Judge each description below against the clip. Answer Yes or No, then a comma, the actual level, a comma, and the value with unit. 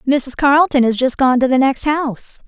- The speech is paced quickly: Yes, fast, 220 wpm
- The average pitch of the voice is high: Yes, very high, 270 Hz